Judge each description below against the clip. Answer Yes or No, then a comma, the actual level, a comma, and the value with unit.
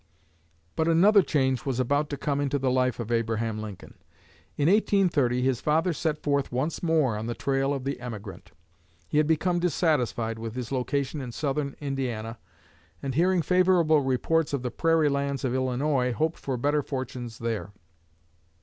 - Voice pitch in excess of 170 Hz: No, low, 135 Hz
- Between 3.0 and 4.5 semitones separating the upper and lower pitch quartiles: Yes, average, 3.9 semitones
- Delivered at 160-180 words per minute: Yes, average, 165 wpm